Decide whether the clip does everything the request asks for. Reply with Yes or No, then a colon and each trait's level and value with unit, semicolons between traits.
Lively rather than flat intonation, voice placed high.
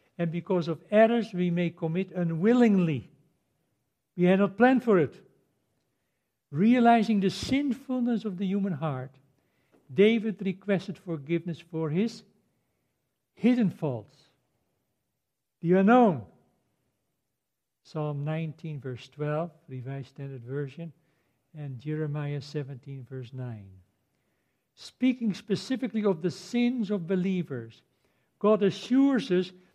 No: wide, 6.7 semitones; medium, 170 Hz